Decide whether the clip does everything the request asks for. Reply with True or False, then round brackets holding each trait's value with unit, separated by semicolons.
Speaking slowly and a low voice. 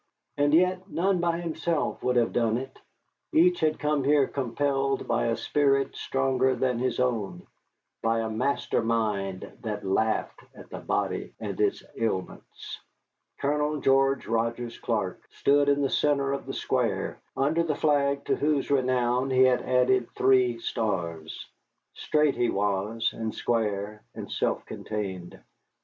False (145 wpm; 130 Hz)